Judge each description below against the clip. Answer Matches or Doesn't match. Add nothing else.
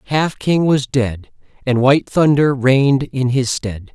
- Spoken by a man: Matches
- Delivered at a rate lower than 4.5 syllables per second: Matches